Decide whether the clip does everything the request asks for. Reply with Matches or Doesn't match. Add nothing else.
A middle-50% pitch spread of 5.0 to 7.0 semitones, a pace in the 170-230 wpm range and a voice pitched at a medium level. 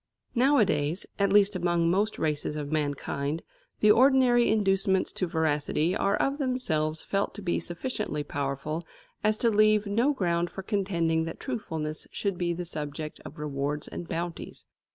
Doesn't match